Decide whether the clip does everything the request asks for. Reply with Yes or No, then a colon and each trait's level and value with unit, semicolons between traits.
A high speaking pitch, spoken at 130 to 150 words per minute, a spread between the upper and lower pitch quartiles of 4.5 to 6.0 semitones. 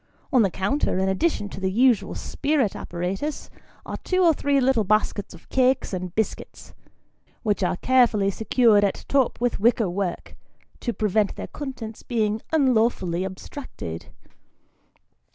Yes: high, 220 Hz; average, 140 wpm; average, 5.2 semitones